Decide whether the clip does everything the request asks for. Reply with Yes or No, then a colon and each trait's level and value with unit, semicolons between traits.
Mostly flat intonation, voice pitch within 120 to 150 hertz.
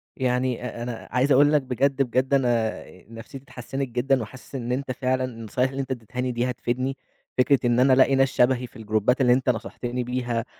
Yes: narrow, 1.7 semitones; low, 125 Hz